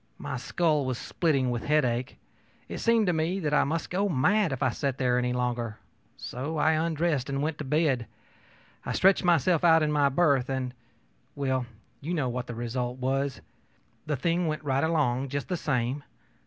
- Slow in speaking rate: No, average, 185 wpm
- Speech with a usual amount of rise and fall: Yes, average, 4.2 semitones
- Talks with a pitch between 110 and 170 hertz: Yes, medium, 140 Hz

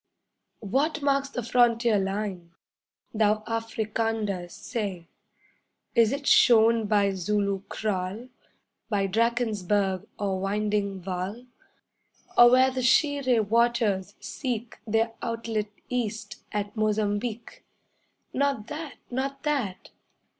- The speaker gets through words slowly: Yes, slow, 100 wpm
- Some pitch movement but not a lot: Yes, average, 3.1 semitones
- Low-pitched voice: No, high, 220 Hz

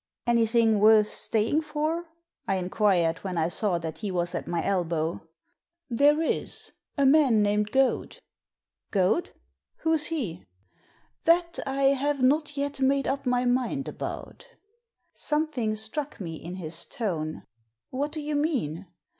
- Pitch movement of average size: No, wide, 7.8 semitones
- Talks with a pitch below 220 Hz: No, high, 235 Hz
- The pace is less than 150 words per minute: Yes, average, 140 wpm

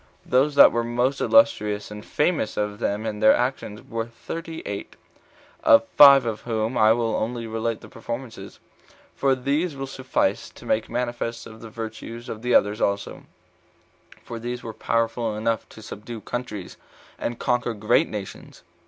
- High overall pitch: No, low, 115 Hz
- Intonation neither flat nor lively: No, narrow, 2.2 semitones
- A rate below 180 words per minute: Yes, average, 160 wpm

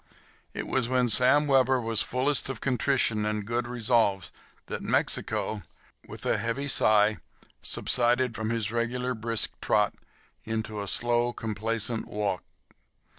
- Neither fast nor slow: No, slow, 130 wpm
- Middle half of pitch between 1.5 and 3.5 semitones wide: Yes, narrow, 2.6 semitones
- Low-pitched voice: Yes, low, 115 Hz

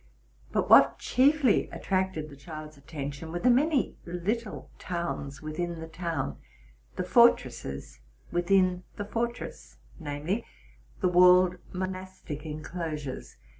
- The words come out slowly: Yes, slow, 115 wpm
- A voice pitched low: No, medium, 175 Hz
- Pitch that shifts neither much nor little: Yes, average, 3.7 semitones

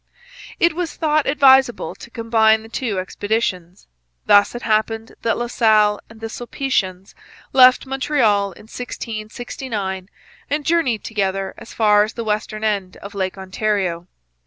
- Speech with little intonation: No, average, 3.3 semitones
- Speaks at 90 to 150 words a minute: Yes, average, 140 wpm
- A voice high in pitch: Yes, high, 220 Hz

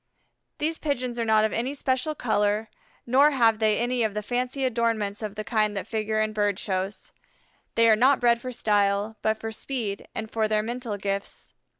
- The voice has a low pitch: No, high, 220 Hz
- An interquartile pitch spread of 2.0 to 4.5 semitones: Yes, narrow, 2.6 semitones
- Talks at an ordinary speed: Yes, average, 195 wpm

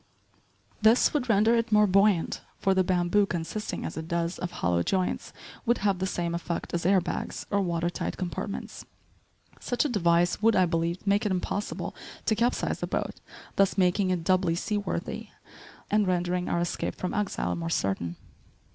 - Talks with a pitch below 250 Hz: Yes, medium, 185 Hz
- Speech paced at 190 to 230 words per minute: No, average, 175 wpm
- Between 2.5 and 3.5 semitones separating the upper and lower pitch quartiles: Yes, average, 3.2 semitones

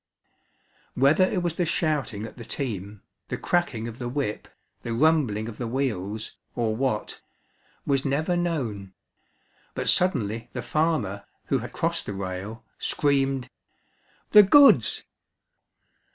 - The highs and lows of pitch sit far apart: Yes, wide, 6.4 semitones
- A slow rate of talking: Yes, slow, 130 wpm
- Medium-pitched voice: No, low, 125 Hz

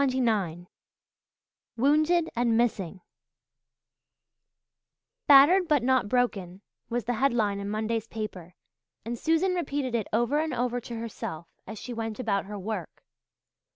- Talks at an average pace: No, slow, 130 wpm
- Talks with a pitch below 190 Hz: No, high, 235 Hz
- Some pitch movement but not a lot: Yes, average, 4.0 semitones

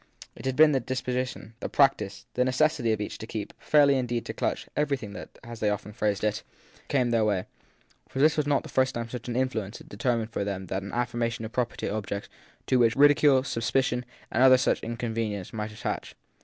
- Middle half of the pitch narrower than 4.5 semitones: Yes, average, 3.4 semitones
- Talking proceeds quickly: Yes, fast, 210 wpm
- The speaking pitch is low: Yes, low, 120 Hz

